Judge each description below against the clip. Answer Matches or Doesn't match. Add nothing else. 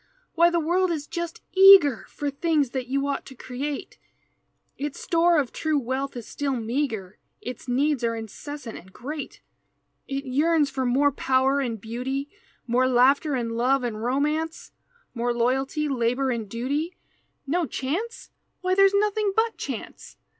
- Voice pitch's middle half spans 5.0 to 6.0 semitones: Doesn't match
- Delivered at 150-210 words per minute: Matches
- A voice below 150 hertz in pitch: Doesn't match